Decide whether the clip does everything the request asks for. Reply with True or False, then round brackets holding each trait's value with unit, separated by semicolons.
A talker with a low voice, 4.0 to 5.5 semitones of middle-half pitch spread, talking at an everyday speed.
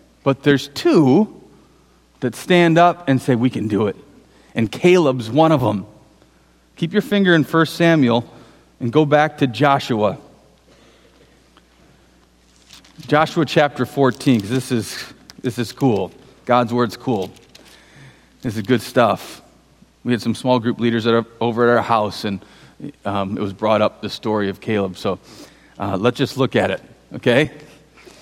True (120 Hz; 5.0 semitones; 155 wpm)